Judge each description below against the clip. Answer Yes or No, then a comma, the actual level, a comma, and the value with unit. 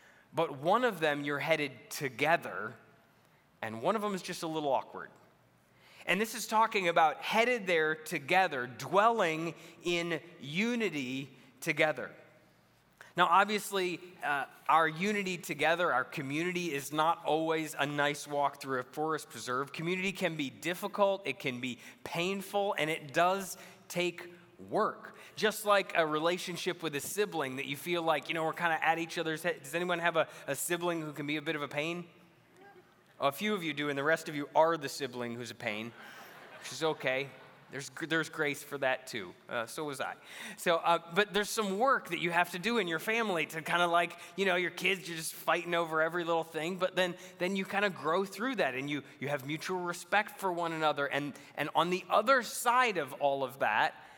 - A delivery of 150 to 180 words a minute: No, average, 200 wpm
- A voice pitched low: No, medium, 165 Hz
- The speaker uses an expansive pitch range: No, average, 3.9 semitones